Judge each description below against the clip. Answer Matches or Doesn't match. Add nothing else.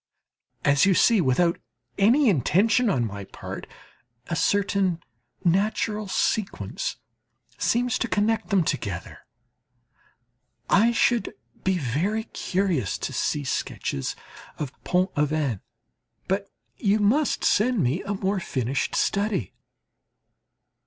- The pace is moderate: Doesn't match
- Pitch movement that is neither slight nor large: Doesn't match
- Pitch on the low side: Doesn't match